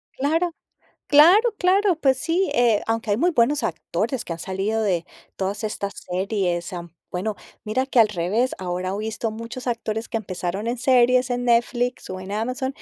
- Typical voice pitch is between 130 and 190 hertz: No, high, 225 Hz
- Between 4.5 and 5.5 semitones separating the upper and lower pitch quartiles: Yes, average, 4.8 semitones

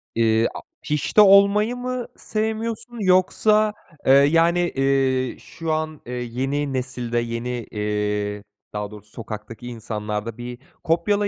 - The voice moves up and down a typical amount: No, wide, 8.3 semitones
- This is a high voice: No, low, 135 Hz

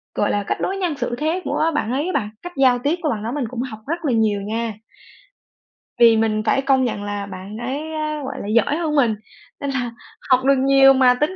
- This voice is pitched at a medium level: No, very high, 260 Hz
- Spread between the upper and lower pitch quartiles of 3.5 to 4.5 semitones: No, average, 4.9 semitones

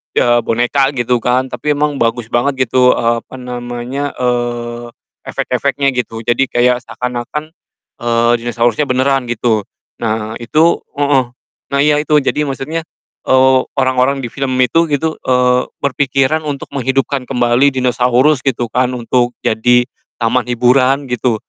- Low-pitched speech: Yes, low, 125 Hz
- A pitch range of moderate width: No, narrow, 2.2 semitones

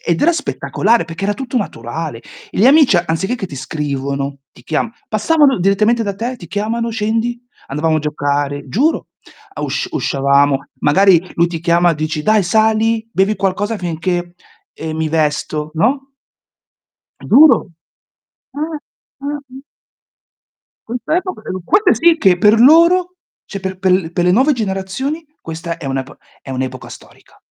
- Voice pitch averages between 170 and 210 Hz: Yes, high, 190 Hz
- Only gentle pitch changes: No, wide, 6.8 semitones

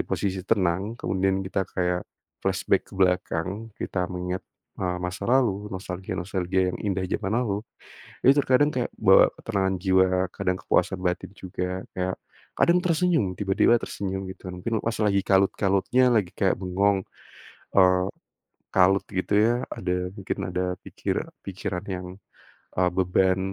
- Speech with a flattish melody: Yes, narrow, 1.6 semitones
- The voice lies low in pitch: Yes, very low, 95 Hz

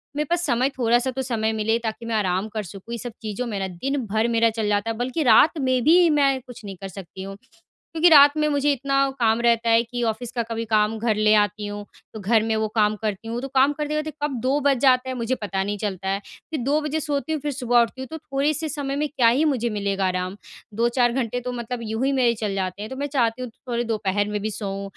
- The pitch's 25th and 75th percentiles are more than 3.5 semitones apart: Yes, average, 4.2 semitones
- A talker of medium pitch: No, high, 235 Hz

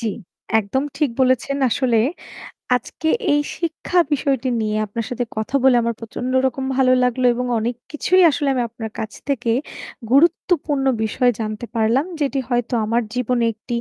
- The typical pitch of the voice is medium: No, very high, 250 Hz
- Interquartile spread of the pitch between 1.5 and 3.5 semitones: Yes, average, 3.1 semitones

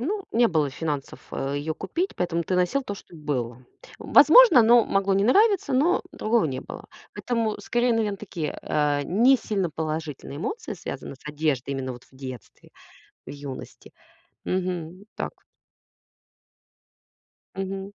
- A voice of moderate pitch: Yes, medium, 180 Hz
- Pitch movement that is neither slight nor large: No, wide, 8.1 semitones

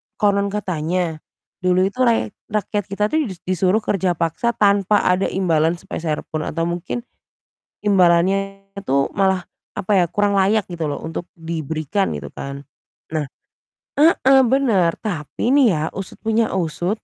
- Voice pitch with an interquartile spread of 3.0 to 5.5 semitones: Yes, average, 3.7 semitones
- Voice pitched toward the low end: No, high, 190 Hz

